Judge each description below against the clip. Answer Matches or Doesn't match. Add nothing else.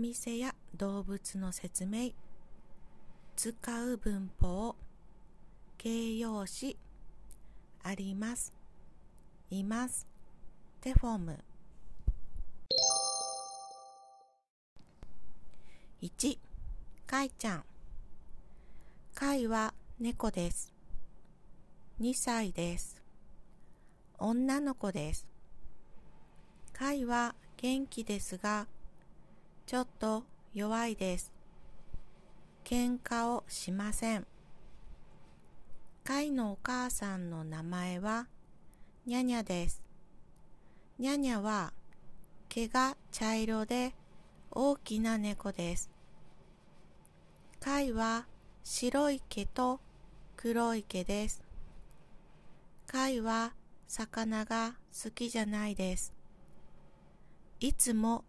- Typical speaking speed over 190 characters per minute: Doesn't match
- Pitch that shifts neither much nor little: Matches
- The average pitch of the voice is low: Doesn't match